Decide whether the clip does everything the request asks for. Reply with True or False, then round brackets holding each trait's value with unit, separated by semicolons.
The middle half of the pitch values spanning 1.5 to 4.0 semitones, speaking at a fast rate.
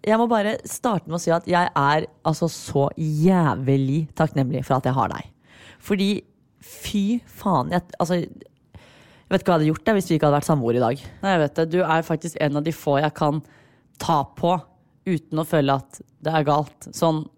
True (3.6 semitones; 215 wpm)